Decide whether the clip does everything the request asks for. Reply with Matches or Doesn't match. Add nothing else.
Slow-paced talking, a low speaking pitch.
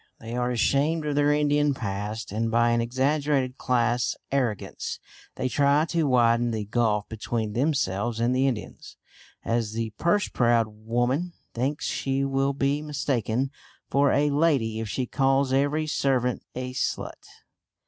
Doesn't match